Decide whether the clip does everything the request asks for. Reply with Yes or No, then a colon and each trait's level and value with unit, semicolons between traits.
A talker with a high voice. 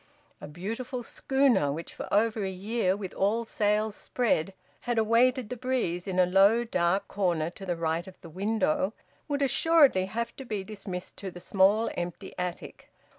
Yes: high, 205 Hz